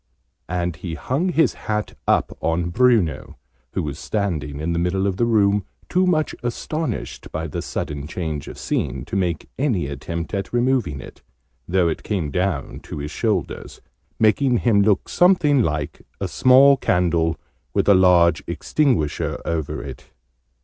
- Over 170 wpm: No, average, 155 wpm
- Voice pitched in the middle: No, very low, 90 Hz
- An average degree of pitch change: No, wide, 6.8 semitones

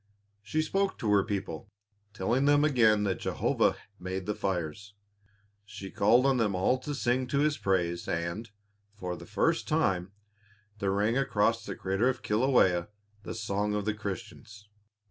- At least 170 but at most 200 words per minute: No, average, 155 wpm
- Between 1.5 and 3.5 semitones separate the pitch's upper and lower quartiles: No, average, 4.3 semitones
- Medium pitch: No, low, 105 Hz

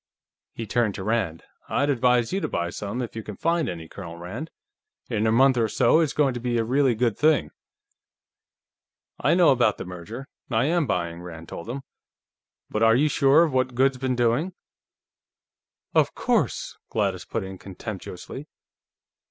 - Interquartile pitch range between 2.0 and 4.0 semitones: No, average, 5.2 semitones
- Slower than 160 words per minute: No, average, 175 wpm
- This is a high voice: No, low, 120 Hz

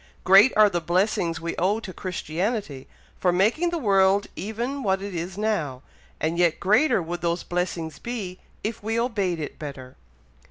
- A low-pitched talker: No, high, 190 Hz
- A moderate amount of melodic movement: Yes, average, 4.2 semitones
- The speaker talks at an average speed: Yes, average, 165 wpm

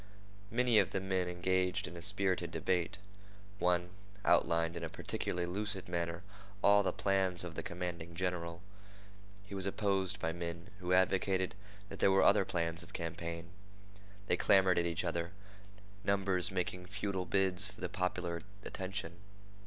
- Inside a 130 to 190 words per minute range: Yes, average, 155 wpm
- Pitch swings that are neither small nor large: No, narrow, 2.1 semitones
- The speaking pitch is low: Yes, very low, 90 Hz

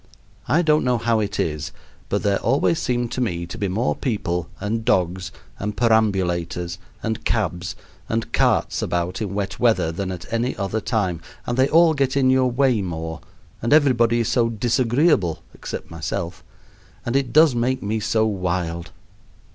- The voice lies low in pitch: Yes, low, 110 Hz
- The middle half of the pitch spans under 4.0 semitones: No, average, 5.3 semitones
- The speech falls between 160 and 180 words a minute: Yes, average, 170 wpm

